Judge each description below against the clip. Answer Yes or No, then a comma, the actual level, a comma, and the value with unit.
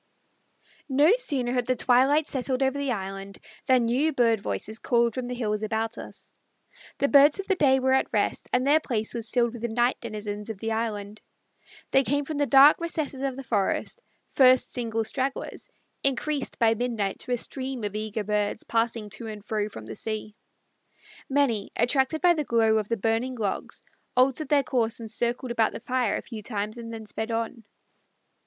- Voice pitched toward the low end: No, high, 235 Hz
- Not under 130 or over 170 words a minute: No, average, 190 wpm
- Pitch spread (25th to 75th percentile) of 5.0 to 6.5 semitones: No, average, 3.4 semitones